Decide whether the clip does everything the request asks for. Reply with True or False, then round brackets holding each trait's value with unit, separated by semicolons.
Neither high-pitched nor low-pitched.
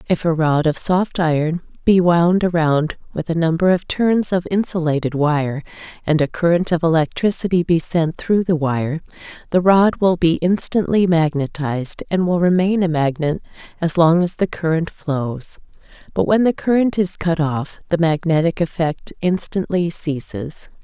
True (170 Hz)